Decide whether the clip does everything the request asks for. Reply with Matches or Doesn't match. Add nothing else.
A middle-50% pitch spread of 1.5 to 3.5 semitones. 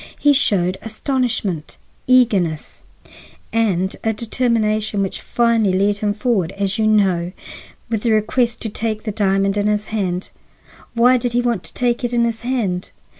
Matches